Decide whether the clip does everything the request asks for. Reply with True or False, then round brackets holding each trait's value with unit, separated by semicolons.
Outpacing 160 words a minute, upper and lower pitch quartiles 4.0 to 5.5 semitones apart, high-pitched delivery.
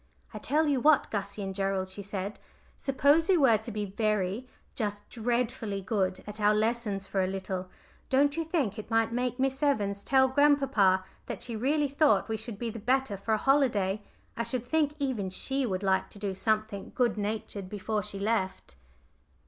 True (190 wpm; 4.8 semitones; 220 Hz)